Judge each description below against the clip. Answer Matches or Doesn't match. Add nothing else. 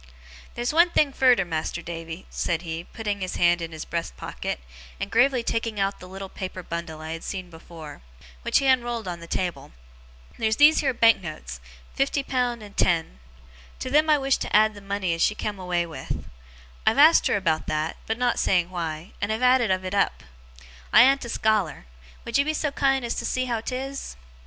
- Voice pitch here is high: Matches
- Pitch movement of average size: Doesn't match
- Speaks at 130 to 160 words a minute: Doesn't match